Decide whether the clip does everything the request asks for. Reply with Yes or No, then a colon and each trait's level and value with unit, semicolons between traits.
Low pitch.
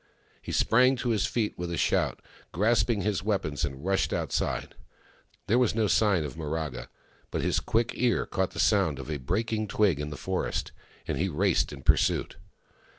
Yes: very low, 95 Hz